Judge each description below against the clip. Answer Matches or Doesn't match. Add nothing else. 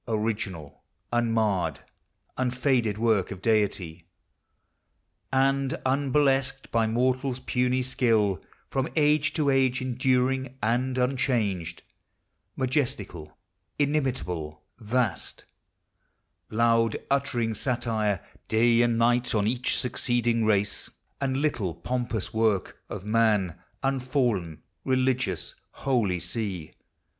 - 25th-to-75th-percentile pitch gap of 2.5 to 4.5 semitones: Matches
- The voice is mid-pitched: Doesn't match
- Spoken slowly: Matches